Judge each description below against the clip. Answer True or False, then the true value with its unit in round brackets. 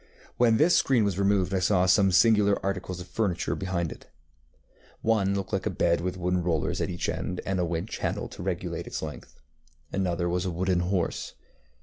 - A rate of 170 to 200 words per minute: True (195 wpm)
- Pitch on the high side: False (95 Hz)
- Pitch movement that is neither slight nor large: False (2.1 semitones)